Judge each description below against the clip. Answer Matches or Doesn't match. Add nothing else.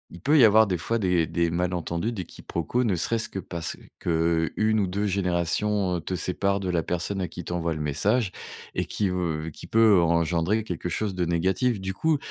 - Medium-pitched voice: Doesn't match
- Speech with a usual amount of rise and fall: Matches